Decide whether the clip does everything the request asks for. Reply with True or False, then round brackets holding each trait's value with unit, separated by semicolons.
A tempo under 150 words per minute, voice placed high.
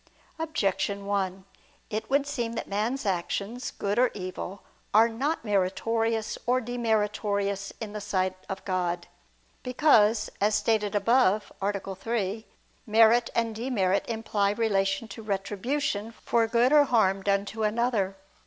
True (135 wpm; 215 Hz)